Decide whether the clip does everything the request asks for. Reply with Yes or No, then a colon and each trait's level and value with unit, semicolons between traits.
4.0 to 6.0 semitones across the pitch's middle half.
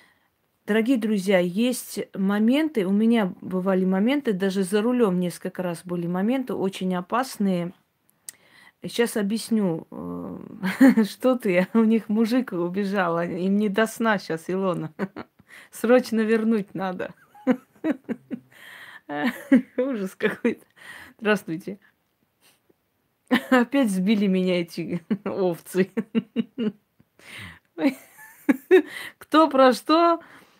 Yes: average, 4.7 semitones